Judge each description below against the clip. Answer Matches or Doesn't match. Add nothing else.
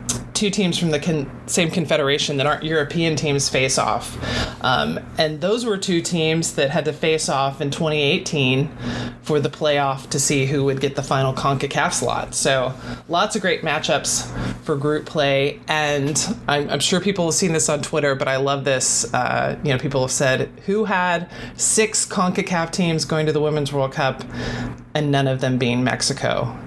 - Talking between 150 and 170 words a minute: Doesn't match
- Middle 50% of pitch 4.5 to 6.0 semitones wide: Doesn't match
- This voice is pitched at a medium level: Matches